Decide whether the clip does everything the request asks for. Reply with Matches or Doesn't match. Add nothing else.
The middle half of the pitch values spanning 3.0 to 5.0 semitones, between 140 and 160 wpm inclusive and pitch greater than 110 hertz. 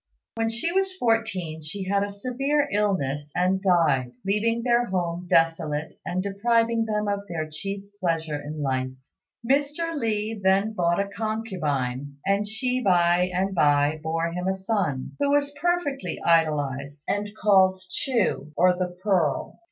Doesn't match